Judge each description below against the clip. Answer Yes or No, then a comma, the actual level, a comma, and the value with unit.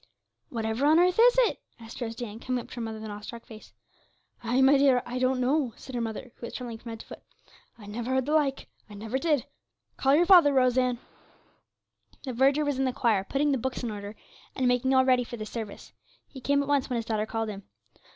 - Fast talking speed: Yes, fast, 240 wpm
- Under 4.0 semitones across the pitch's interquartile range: Yes, average, 3.3 semitones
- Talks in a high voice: Yes, very high, 250 Hz